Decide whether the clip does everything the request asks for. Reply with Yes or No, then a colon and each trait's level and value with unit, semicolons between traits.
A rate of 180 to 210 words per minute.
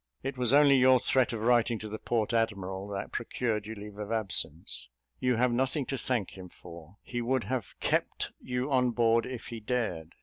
Yes: average, 200 wpm